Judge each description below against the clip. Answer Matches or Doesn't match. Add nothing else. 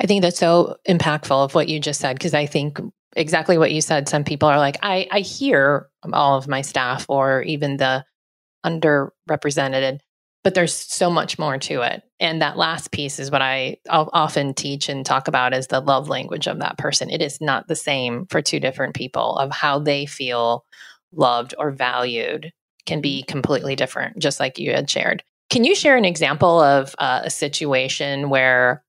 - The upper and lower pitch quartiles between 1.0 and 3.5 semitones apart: Matches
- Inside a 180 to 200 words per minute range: Matches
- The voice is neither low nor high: Matches